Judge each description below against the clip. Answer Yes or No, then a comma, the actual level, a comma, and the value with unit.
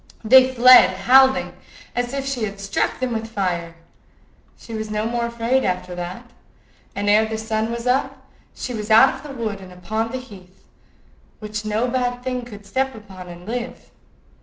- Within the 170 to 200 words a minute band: Yes, average, 180 wpm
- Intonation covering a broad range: No, average, 3.5 semitones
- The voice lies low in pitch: No, high, 225 Hz